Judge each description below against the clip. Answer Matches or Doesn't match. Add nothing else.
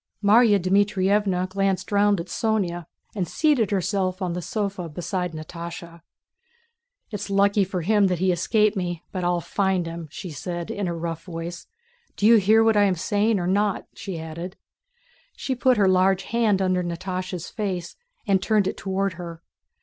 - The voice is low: Doesn't match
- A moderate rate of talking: Matches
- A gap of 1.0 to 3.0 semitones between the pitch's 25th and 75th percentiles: Matches